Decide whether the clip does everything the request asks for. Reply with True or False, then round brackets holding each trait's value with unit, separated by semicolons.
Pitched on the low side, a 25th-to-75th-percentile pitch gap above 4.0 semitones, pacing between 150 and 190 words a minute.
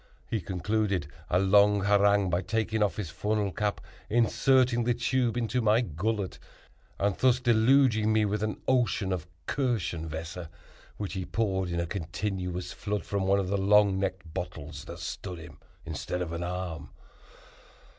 False (100 Hz; 3.4 semitones; 155 wpm)